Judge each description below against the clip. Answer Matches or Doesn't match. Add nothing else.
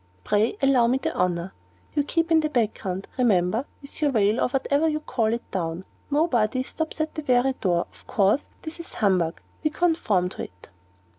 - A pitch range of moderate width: Doesn't match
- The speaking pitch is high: Matches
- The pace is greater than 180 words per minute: Matches